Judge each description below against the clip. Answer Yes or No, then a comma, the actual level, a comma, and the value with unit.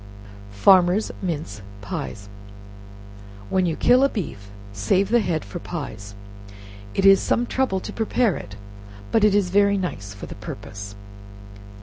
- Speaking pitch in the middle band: Yes, medium, 180 Hz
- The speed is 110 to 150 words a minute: Yes, average, 140 wpm